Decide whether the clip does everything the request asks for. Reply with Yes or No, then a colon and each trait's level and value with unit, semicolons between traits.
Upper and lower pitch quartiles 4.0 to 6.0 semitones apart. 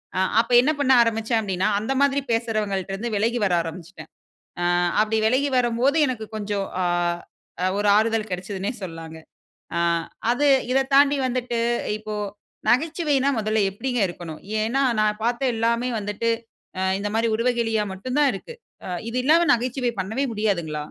No: average, 3.6 semitones